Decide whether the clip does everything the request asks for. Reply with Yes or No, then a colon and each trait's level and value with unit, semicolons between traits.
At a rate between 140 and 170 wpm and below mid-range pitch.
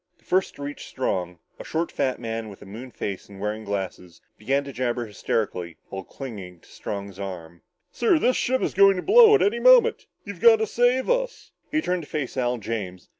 No: fast, 205 wpm; low, 125 Hz